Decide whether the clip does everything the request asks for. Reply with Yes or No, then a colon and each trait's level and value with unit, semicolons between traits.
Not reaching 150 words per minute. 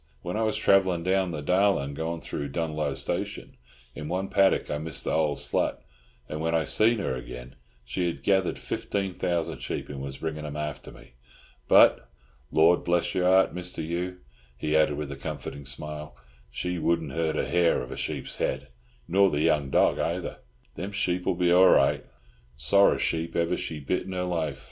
No: average, 185 wpm